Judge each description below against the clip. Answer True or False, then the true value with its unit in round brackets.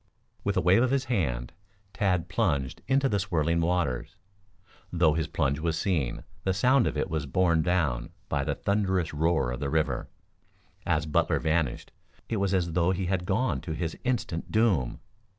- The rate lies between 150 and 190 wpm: True (175 wpm)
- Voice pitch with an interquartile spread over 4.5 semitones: False (3.9 semitones)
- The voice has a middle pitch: False (85 Hz)